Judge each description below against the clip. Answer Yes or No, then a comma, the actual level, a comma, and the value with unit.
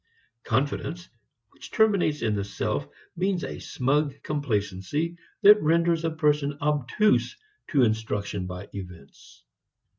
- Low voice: No, medium, 145 Hz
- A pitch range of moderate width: No, wide, 8.0 semitones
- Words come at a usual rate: No, slow, 115 wpm